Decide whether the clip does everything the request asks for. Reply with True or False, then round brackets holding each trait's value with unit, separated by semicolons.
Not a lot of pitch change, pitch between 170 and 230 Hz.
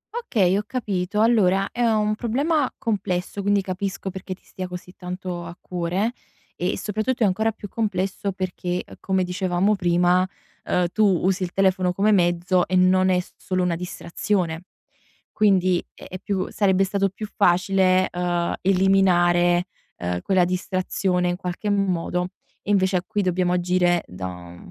True (2.0 semitones; 185 Hz)